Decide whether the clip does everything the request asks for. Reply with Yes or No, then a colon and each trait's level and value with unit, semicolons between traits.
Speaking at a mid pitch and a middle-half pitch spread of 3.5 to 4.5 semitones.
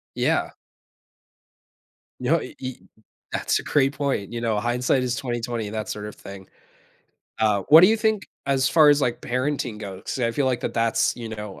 No: low, 125 Hz; average, 4.1 semitones